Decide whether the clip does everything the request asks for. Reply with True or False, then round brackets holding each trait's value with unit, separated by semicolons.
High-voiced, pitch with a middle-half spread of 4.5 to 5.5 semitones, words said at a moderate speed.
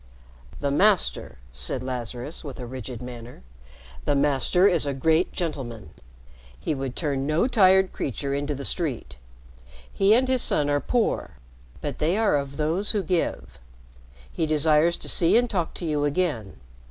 False (150 Hz; 5.2 semitones; 160 wpm)